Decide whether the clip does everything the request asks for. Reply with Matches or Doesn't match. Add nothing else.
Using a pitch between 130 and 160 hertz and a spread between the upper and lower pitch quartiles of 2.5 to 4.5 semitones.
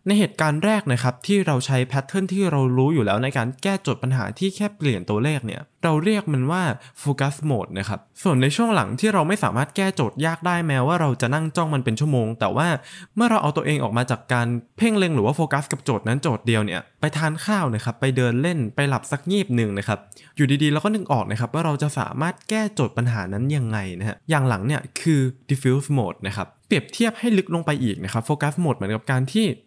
Doesn't match